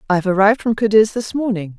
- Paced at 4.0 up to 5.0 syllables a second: No, 6.8 syllables/s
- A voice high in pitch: Yes, high, 205 Hz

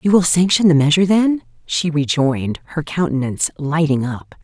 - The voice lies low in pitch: No, medium, 155 Hz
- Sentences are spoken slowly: No, average, 160 wpm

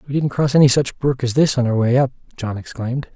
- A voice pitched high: No, low, 130 Hz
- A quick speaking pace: Yes, fast, 265 wpm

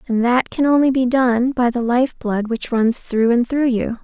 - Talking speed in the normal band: No, fast, 240 wpm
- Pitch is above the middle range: Yes, high, 245 Hz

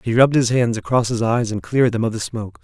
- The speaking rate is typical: No, fast, 295 wpm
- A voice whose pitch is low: Yes, low, 115 Hz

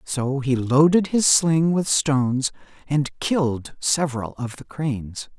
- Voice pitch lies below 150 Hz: Yes, medium, 140 Hz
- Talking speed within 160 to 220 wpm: No, average, 145 wpm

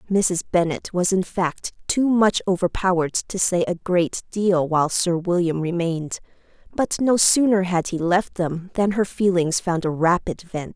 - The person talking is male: No, female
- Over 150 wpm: Yes, average, 175 wpm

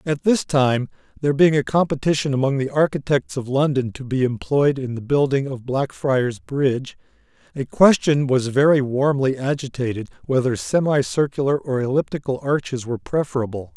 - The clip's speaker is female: No, male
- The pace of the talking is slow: No, average, 150 wpm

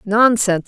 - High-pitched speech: Yes, high, 210 Hz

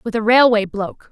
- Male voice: No, female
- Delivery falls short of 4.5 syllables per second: No, 5.9 syllables/s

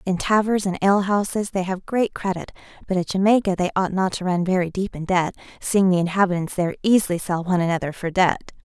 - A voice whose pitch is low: No, medium, 185 Hz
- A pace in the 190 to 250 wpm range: Yes, fast, 205 wpm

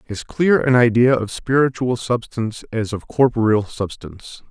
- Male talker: Yes, male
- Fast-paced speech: No, average, 145 wpm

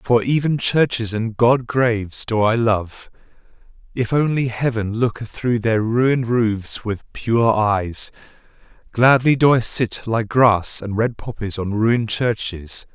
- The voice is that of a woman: No, male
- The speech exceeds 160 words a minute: No, average, 145 wpm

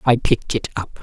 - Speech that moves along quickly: Yes, fast, 235 wpm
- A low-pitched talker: Yes, low, 115 Hz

